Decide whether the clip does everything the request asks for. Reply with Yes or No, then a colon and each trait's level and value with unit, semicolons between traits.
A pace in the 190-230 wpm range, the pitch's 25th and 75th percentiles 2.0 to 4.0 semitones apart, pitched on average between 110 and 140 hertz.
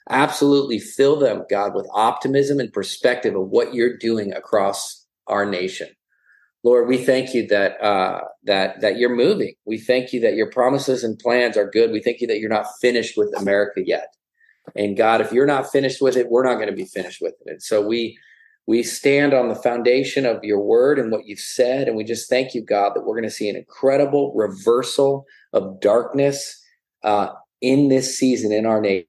Yes: fast, 205 wpm; average, 3.4 semitones; low, 125 Hz